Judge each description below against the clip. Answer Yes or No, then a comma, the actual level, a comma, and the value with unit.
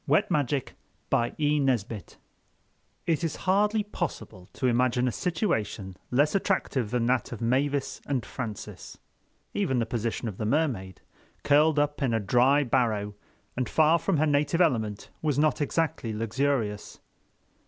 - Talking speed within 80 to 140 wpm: Yes, slow, 135 wpm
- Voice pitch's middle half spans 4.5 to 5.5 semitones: Yes, average, 4.8 semitones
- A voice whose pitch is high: No, low, 130 Hz